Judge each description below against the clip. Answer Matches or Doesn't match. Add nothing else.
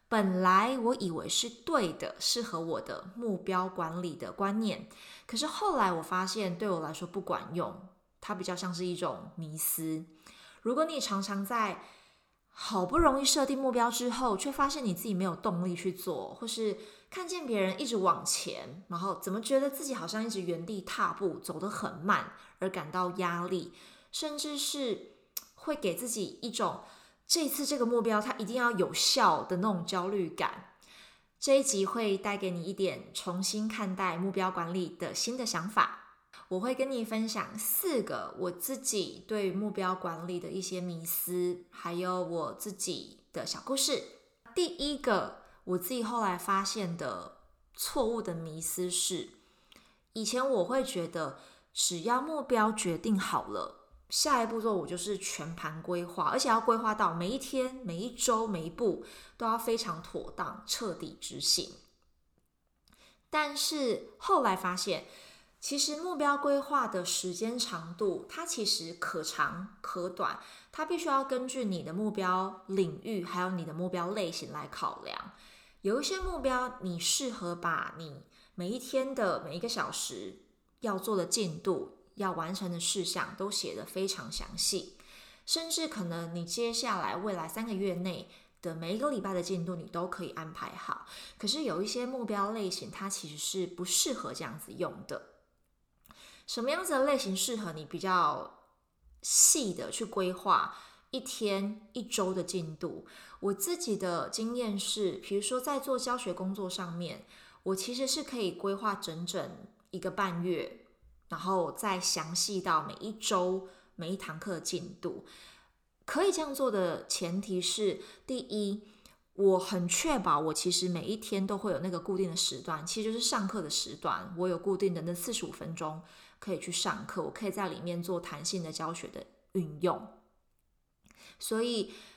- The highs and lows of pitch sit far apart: Doesn't match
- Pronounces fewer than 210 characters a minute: Doesn't match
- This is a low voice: Doesn't match